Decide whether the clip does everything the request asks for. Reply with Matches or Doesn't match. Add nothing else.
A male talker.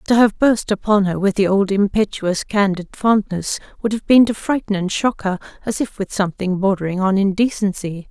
Doesn't match